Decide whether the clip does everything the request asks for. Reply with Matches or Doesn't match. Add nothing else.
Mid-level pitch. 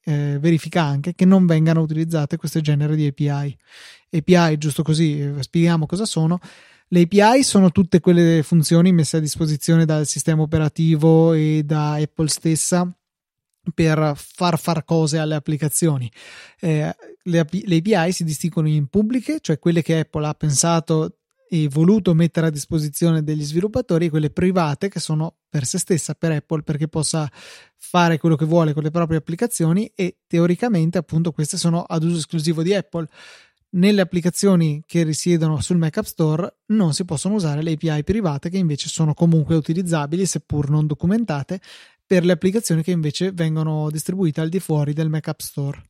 Matches